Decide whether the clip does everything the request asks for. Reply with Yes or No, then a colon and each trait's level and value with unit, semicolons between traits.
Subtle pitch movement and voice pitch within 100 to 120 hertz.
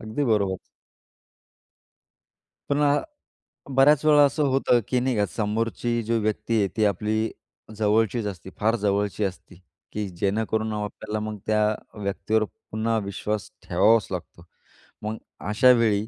Yes: narrow, 2.0 semitones; low, 110 Hz